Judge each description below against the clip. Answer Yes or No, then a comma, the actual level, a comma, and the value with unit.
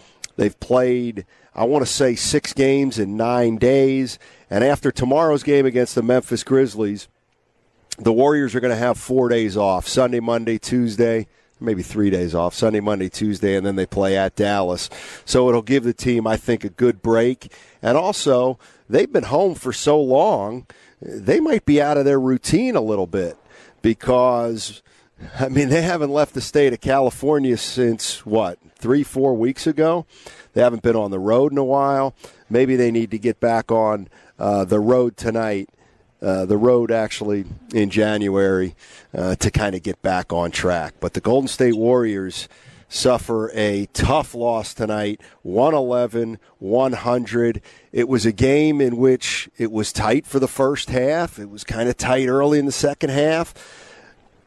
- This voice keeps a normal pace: Yes, average, 175 wpm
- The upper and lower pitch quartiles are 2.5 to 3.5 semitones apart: No, average, 3.9 semitones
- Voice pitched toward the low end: Yes, low, 120 Hz